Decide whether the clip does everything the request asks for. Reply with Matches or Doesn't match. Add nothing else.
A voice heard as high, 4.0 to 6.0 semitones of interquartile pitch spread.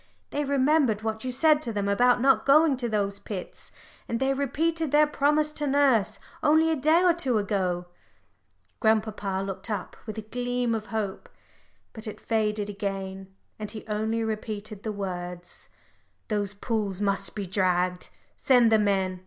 Matches